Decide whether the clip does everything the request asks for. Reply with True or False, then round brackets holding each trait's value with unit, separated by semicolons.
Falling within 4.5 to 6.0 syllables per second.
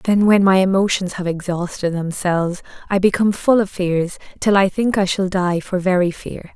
True (5.1 syllables/s)